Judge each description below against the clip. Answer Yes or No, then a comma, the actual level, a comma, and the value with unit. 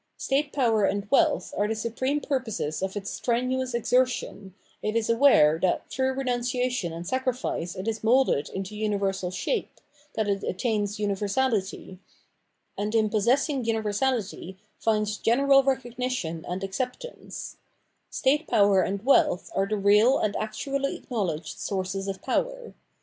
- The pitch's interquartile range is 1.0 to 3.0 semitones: No, average, 4.7 semitones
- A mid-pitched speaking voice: No, high, 220 Hz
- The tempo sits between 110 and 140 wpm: Yes, slow, 135 wpm